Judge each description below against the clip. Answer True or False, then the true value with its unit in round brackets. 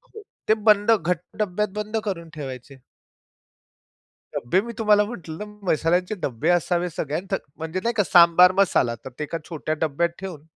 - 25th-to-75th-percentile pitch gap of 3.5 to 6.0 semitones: True (4.6 semitones)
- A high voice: False (175 Hz)